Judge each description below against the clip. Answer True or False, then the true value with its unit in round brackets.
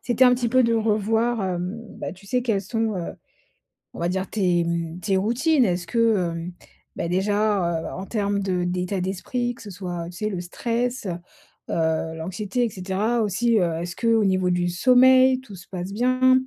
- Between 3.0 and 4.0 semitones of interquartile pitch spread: False (4.6 semitones)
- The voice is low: False (200 Hz)